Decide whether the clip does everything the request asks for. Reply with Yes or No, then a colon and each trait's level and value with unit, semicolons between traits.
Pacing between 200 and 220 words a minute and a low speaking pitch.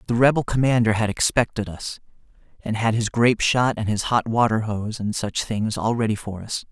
Yes: fast, 205 wpm; low, 110 Hz